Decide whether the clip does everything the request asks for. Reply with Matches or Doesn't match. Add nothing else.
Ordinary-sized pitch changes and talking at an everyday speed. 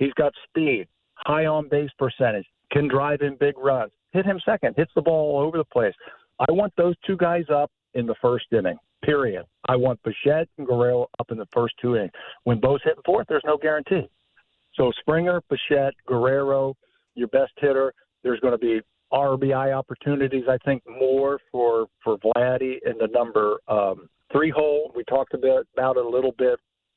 Matches